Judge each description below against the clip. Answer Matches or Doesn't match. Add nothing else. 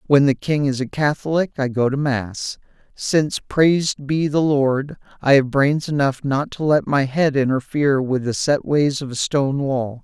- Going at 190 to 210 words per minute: Matches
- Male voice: Matches